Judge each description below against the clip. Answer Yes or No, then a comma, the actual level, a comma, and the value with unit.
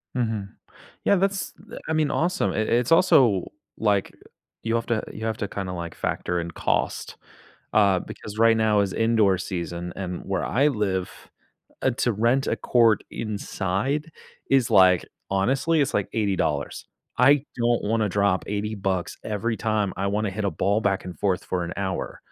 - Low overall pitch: Yes, low, 105 Hz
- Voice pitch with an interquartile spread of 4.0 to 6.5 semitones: No, average, 3.6 semitones